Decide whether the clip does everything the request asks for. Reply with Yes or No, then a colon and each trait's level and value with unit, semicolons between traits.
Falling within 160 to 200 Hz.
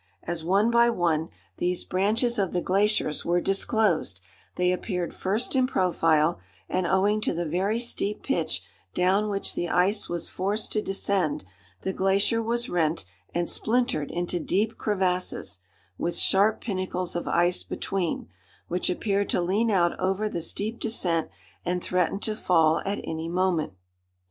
Yes: medium, 185 Hz